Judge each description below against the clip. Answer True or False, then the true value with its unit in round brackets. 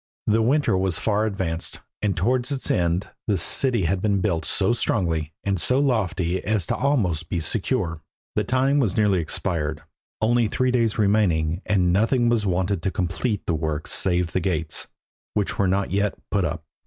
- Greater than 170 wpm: True (180 wpm)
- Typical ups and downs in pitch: True (4.3 semitones)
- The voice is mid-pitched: False (100 Hz)